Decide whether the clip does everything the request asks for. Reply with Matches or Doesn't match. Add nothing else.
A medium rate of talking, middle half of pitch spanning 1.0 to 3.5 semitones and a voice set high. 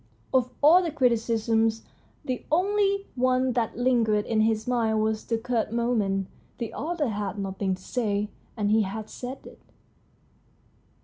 Matches